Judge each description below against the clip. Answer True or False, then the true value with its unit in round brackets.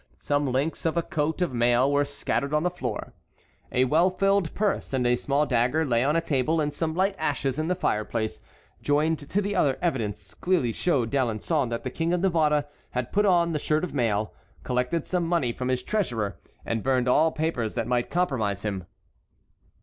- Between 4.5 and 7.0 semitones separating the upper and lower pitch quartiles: True (5.2 semitones)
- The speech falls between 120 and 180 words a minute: False (195 wpm)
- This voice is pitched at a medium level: True (145 Hz)